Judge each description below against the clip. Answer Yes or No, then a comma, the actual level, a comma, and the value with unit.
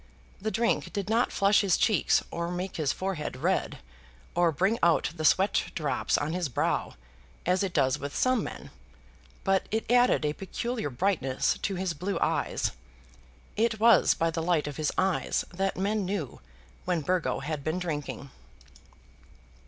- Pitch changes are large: No, average, 4.3 semitones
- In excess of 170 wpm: No, average, 160 wpm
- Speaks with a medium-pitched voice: Yes, medium, 180 Hz